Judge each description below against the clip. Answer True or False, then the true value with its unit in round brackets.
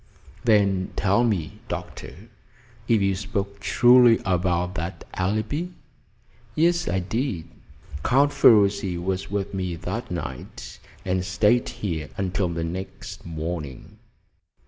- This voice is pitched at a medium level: False (95 Hz)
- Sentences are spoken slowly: True (115 wpm)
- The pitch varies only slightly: False (3.5 semitones)